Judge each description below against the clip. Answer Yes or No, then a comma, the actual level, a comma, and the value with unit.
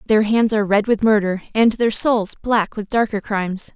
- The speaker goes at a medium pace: No, fast, 210 wpm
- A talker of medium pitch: No, high, 215 Hz